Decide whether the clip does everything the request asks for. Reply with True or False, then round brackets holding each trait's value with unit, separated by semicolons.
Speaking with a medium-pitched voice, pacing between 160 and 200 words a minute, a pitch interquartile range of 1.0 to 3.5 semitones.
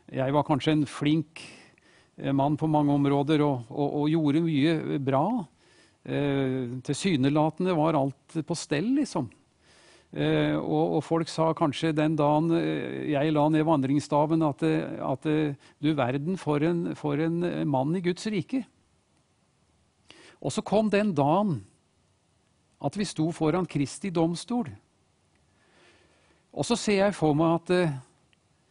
False (155 Hz; 135 wpm; 2.7 semitones)